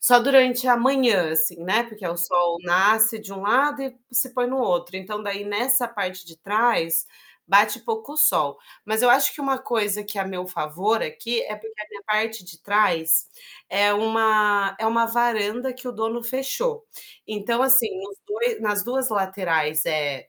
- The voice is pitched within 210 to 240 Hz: Yes, high, 215 Hz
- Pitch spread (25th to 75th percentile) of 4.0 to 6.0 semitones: Yes, average, 4.3 semitones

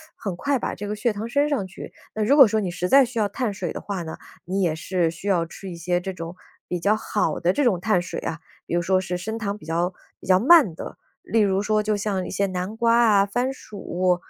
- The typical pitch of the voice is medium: No, high, 195 Hz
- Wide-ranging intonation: No, average, 3.5 semitones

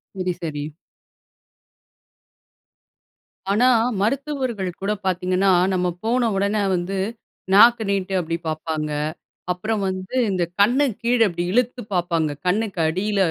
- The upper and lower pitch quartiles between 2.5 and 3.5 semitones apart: No, average, 3.9 semitones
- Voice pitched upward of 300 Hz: No, high, 195 Hz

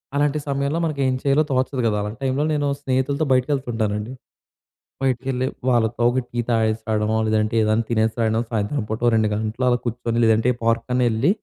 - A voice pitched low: Yes, low, 120 Hz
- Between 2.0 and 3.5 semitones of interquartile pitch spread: Yes, average, 3.1 semitones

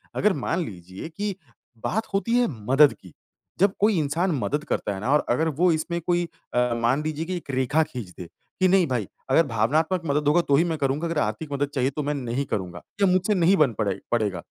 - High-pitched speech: No, medium, 150 Hz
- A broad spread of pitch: Yes, wide, 5.9 semitones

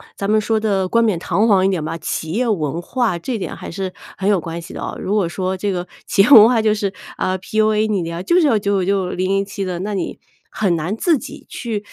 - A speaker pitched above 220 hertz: No, high, 195 Hz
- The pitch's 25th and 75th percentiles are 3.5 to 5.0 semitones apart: No, average, 2.9 semitones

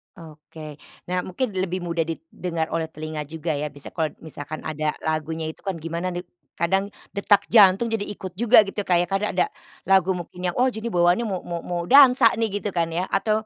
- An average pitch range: Yes, average, 3.5 semitones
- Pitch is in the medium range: Yes, medium, 175 Hz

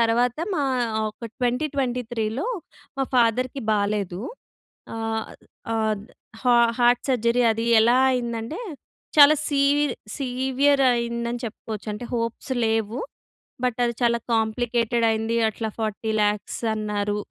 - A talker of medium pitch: No, high, 235 Hz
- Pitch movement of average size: No, narrow, 2.1 semitones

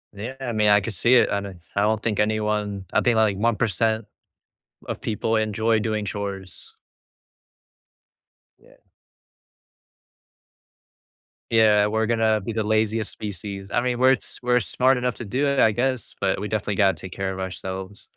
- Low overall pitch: Yes, low, 110 Hz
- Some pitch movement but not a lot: No, narrow, 2.2 semitones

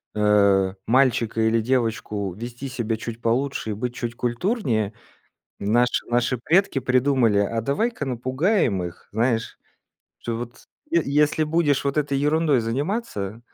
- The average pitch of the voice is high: No, low, 120 Hz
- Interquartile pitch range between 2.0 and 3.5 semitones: No, average, 3.9 semitones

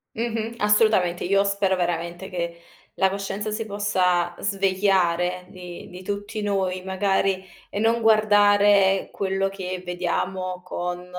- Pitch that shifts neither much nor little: No, narrow, 2.1 semitones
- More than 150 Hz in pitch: Yes, high, 190 Hz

